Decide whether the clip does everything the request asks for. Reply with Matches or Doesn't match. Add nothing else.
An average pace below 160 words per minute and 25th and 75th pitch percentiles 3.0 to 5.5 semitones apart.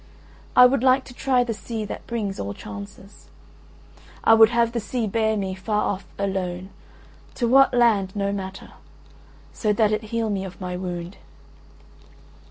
Doesn't match